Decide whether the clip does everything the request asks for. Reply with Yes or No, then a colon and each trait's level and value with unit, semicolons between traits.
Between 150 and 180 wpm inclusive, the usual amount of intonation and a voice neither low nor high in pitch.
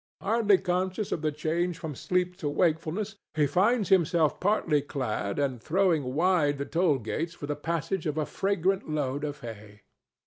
Yes: average, 170 wpm; average, 4.1 semitones; medium, 160 Hz